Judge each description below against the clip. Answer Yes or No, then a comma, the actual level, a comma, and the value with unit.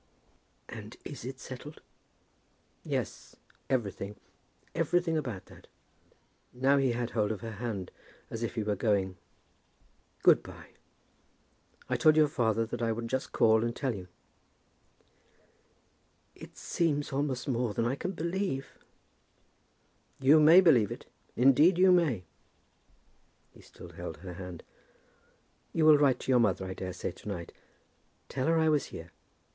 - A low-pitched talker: Yes, low, 125 Hz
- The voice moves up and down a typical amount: No, wide, 5.8 semitones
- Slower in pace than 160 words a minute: Yes, average, 140 wpm